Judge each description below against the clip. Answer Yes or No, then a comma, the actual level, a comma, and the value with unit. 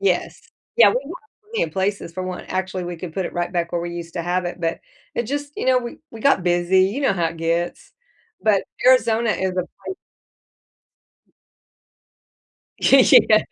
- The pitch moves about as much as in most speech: Yes, average, 4.9 semitones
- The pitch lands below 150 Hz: No, medium, 185 Hz